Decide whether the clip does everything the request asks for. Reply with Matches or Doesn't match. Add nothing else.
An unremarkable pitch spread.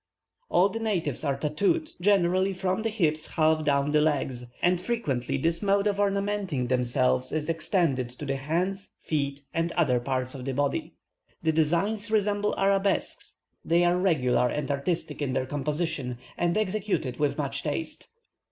Doesn't match